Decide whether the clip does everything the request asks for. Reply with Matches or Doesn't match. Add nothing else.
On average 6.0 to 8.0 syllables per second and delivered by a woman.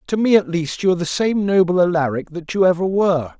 Doesn't match